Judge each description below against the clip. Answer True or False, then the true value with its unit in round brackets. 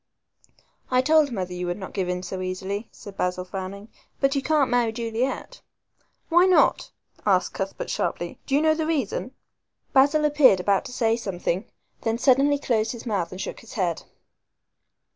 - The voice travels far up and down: True (6.5 semitones)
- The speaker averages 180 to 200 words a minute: False (165 wpm)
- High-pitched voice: True (230 Hz)